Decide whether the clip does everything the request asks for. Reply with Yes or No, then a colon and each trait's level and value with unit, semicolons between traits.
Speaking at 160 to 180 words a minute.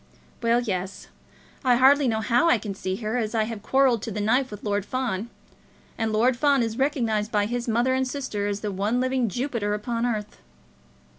No: average, 200 wpm